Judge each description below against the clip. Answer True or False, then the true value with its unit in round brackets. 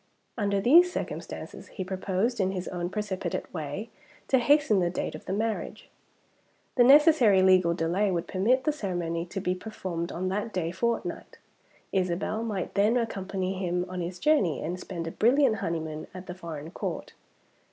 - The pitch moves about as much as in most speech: True (3.9 semitones)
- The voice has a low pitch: False (190 Hz)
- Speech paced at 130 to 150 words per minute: False (165 wpm)